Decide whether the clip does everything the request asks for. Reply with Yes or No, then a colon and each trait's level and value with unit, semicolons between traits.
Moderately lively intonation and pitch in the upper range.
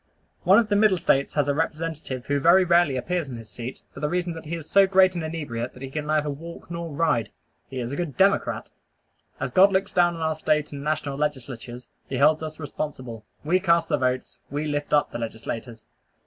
No: average, 4.0 semitones; medium, 150 Hz